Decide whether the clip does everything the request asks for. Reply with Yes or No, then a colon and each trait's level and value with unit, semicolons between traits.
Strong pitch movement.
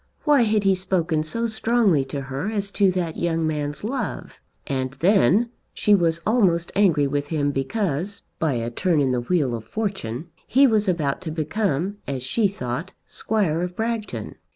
Yes: wide, 6.3 semitones